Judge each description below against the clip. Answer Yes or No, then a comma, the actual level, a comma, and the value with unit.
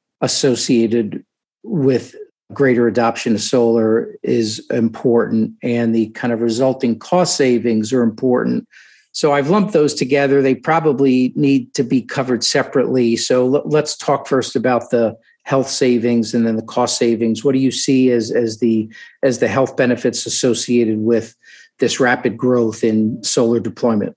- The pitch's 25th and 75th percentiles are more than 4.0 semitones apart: No, average, 2.9 semitones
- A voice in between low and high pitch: No, low, 120 Hz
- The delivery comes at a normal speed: Yes, average, 150 wpm